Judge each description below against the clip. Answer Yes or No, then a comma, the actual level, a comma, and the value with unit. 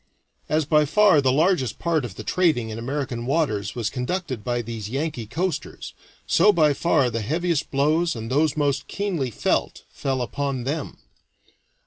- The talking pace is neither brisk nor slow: Yes, average, 160 wpm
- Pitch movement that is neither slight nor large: Yes, average, 4.8 semitones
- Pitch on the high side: No, medium, 140 Hz